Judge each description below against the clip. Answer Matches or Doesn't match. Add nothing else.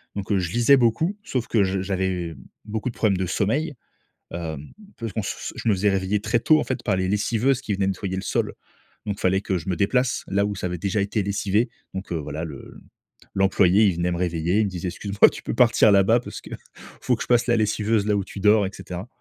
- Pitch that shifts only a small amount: Doesn't match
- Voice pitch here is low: Matches